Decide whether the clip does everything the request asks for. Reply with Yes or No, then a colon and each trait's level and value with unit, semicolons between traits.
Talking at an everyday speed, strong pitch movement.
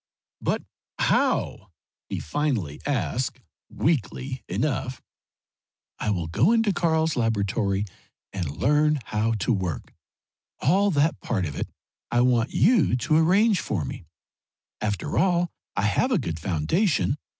No: slow, 130 wpm; wide, 7.9 semitones